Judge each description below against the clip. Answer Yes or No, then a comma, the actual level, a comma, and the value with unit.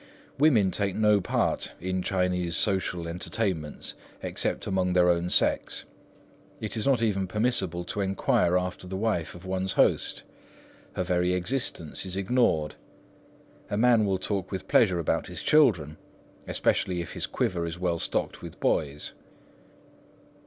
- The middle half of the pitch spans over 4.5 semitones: No, average, 2.7 semitones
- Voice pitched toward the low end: Yes, very low, 95 Hz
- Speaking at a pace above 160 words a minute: No, average, 145 wpm